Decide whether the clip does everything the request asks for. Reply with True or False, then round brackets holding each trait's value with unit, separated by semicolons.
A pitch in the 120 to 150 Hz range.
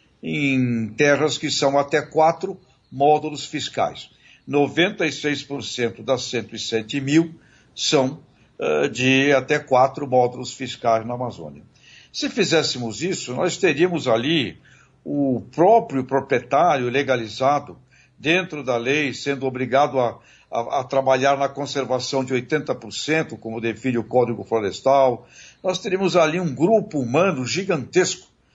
True (135 Hz)